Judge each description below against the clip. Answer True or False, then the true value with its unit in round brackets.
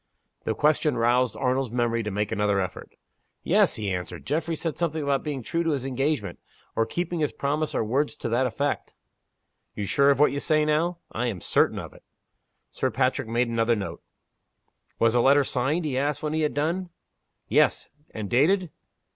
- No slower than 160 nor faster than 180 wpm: False (190 wpm)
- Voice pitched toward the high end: False (135 Hz)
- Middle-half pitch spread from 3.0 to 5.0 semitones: True (4.7 semitones)